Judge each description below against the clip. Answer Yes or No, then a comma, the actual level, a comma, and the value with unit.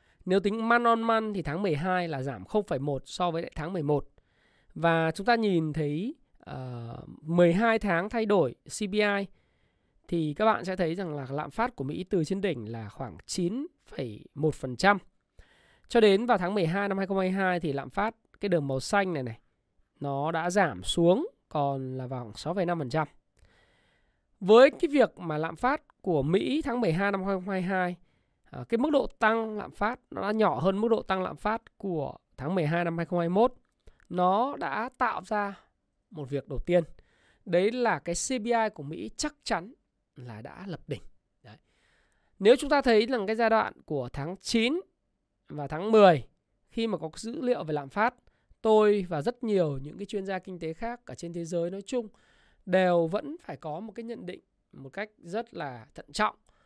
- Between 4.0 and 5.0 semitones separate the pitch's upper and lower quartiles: No, wide, 5.6 semitones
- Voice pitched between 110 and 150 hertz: No, medium, 185 Hz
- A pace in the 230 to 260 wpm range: No, average, 185 wpm